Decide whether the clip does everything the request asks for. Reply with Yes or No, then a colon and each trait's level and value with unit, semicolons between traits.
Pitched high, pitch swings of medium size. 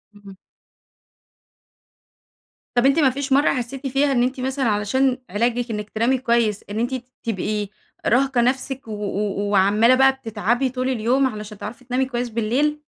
Yes: high, 245 Hz; average, 3.7 semitones